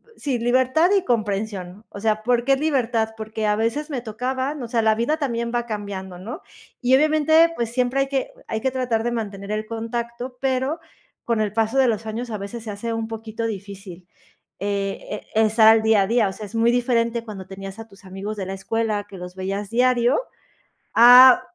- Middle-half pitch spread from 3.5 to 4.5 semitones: No, average, 3.0 semitones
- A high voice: Yes, high, 225 Hz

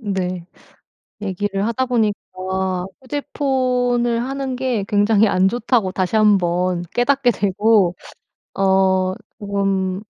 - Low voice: No, high, 205 Hz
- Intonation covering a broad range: No, average, 4.4 semitones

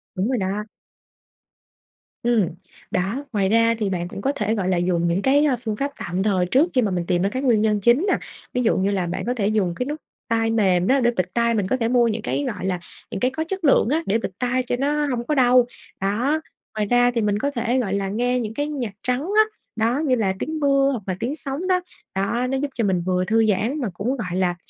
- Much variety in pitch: No, average, 5.0 semitones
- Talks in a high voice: Yes, high, 230 Hz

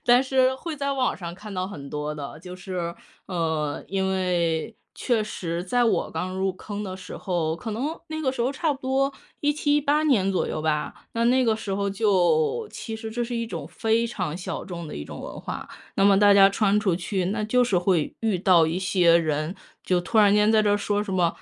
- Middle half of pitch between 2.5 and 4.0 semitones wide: No, average, 4.8 semitones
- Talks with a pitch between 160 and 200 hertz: Yes, high, 195 Hz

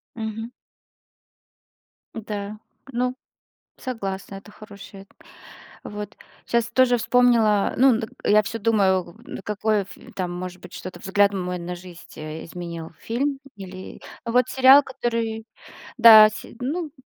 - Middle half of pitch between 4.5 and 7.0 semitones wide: No, average, 3.7 semitones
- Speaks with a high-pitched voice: Yes, high, 215 Hz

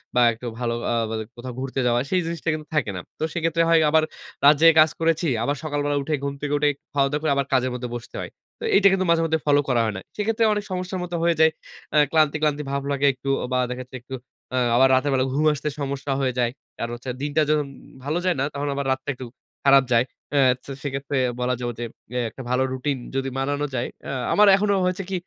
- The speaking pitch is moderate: Yes, medium, 145 Hz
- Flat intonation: No, average, 3.5 semitones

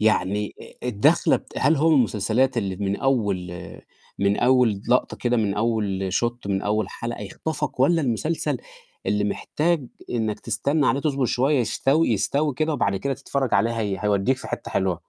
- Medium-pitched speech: No, low, 120 Hz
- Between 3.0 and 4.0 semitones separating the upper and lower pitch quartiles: No, average, 5.0 semitones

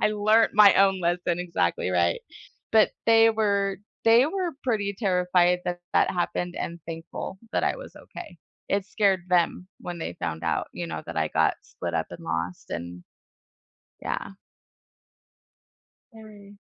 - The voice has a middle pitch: Yes, medium, 180 Hz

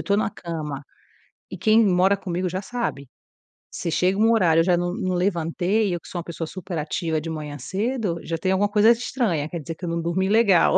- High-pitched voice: No, medium, 180 Hz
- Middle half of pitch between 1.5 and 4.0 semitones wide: Yes, average, 3.6 semitones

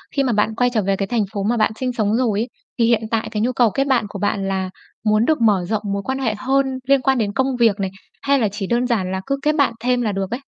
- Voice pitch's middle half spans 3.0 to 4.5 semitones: Yes, average, 3.8 semitones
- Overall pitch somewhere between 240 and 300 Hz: No, high, 225 Hz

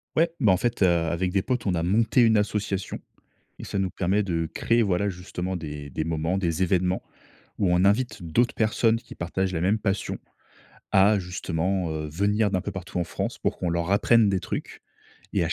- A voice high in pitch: No, very low, 95 Hz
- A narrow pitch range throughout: No, average, 3.2 semitones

